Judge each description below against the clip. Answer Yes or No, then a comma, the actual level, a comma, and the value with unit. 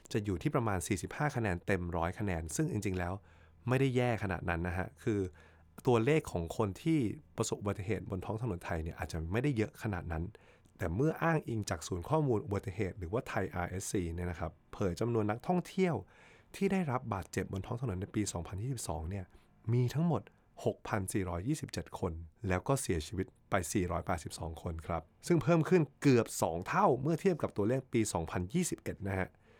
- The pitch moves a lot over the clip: Yes, wide, 5.7 semitones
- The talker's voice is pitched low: Yes, low, 105 Hz